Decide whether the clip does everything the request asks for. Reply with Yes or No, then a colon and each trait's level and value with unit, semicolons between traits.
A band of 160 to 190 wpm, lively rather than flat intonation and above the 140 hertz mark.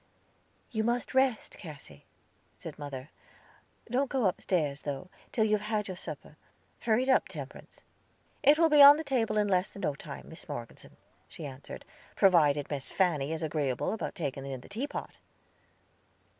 Yes: average, 165 wpm; wide, 7.9 semitones; medium, 185 Hz